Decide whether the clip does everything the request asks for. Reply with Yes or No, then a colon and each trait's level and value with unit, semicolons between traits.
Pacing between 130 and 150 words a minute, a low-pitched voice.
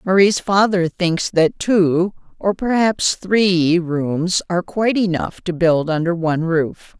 No: average, 145 wpm; medium, 180 Hz